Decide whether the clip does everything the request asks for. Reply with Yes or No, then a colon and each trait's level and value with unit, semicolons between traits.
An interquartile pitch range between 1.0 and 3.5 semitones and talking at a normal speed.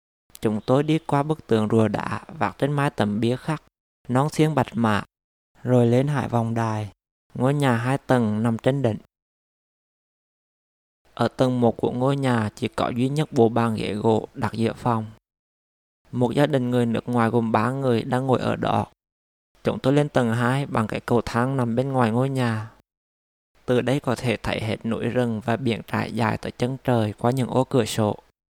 Yes: narrow, 2.6 semitones; average, 200 wpm